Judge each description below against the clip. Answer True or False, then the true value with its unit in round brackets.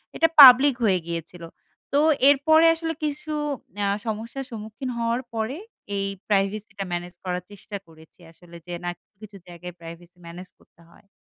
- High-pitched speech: True (205 Hz)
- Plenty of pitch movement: True (6.0 semitones)